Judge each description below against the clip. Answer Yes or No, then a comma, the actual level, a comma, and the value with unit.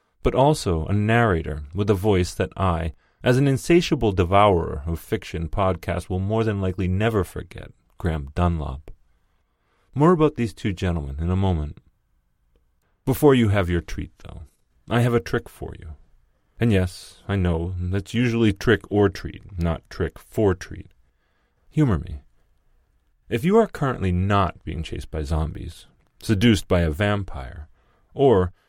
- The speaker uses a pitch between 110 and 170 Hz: No, very low, 95 Hz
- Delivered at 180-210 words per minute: No, average, 155 wpm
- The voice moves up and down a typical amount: Yes, average, 4.7 semitones